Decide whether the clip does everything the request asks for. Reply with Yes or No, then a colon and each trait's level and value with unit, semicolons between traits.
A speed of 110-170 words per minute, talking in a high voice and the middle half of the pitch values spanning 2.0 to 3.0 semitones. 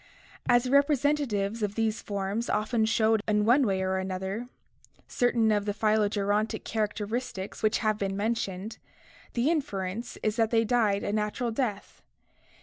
Yes: average, 150 wpm; high, 215 Hz; narrow, 2.5 semitones